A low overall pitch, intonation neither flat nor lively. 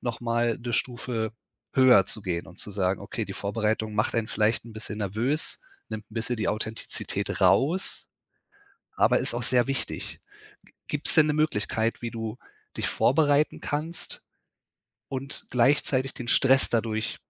Yes: low, 115 Hz; average, 3.5 semitones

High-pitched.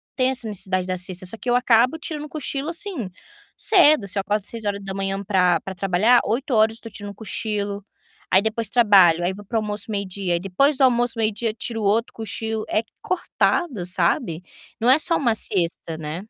Yes: high, 215 Hz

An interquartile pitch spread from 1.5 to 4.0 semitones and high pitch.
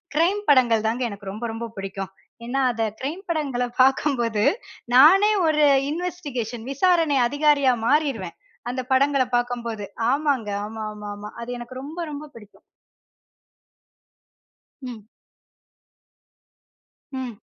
No: average, 4.6 semitones; very high, 255 Hz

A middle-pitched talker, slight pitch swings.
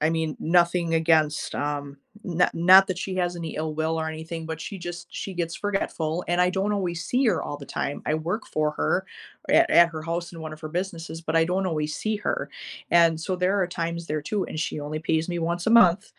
Yes: medium, 170 Hz; narrow, 2.3 semitones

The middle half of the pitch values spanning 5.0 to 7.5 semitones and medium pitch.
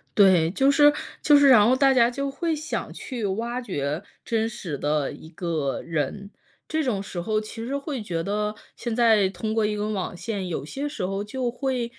No: wide, 5.4 semitones; high, 215 Hz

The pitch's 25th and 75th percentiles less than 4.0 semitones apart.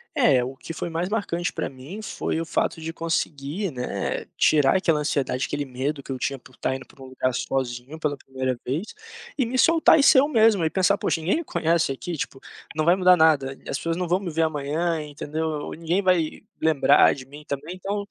No: average, 4.6 semitones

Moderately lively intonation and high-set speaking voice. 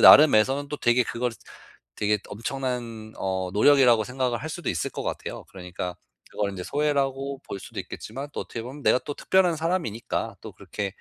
No: average, 4.9 semitones; low, 125 Hz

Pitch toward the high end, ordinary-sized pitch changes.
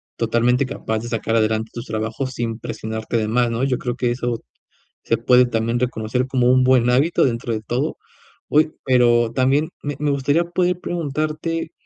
No: low, 125 Hz; average, 3.1 semitones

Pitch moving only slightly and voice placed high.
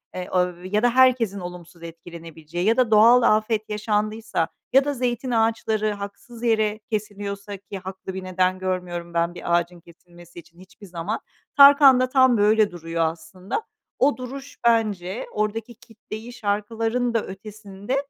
No: average, 4.1 semitones; high, 210 Hz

